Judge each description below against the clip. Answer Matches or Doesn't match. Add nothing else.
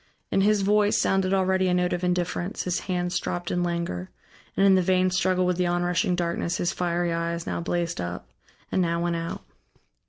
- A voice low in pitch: Doesn't match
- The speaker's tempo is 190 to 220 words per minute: Matches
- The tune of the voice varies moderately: Doesn't match